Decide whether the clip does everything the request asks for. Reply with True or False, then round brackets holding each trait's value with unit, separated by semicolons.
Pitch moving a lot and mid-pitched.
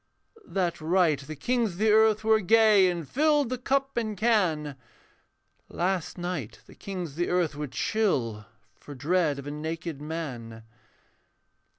True (6.4 semitones; 175 Hz)